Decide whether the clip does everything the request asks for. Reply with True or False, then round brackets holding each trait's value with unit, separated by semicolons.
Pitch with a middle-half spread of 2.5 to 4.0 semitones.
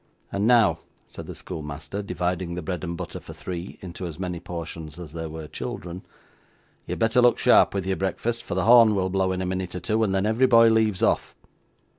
True (3.7 semitones)